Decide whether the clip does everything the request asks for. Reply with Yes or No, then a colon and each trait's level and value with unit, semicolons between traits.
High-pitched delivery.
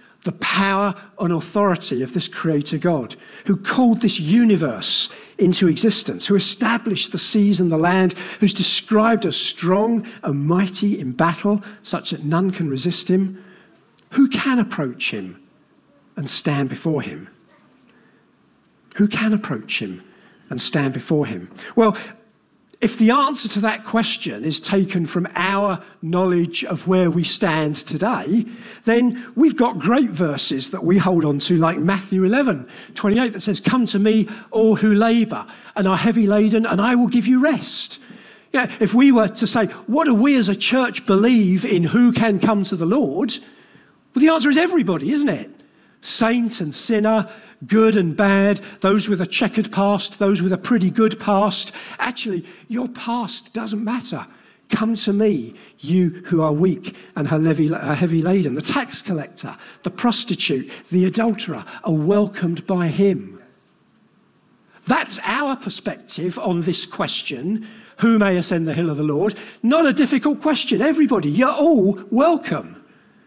Yes: high, 205 Hz